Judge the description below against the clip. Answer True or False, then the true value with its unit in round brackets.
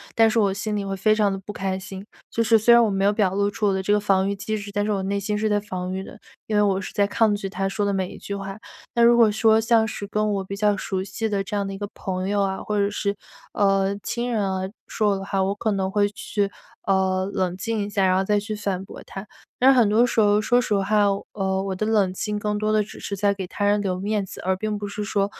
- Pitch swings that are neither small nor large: False (1.6 semitones)